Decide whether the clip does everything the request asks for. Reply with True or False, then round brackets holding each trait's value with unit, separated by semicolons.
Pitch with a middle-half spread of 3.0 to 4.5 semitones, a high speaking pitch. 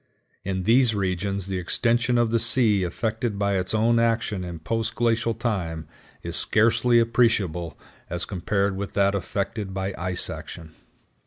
False (3.7 semitones; 100 Hz)